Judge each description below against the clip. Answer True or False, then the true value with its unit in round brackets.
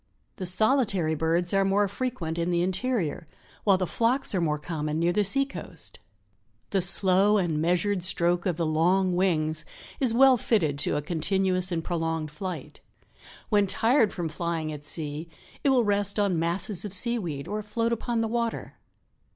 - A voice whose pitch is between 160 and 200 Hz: True (185 Hz)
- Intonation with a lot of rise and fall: False (4.2 semitones)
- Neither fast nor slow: True (170 wpm)